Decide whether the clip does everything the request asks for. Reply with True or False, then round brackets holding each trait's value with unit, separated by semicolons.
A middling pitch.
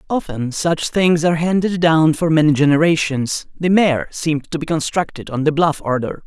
True (160 Hz)